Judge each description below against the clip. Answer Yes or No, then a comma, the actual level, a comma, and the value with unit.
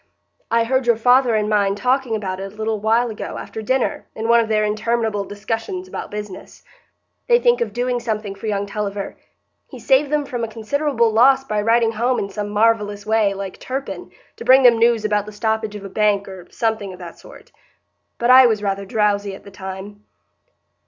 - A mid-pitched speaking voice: No, high, 220 Hz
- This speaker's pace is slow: No, average, 200 wpm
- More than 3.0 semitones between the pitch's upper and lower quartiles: No, average, 2.7 semitones